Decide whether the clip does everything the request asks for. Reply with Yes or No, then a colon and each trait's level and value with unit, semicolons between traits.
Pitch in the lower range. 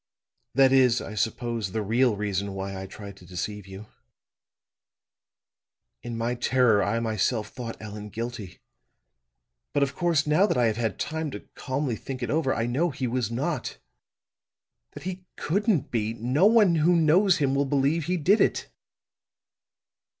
Yes: low, 125 Hz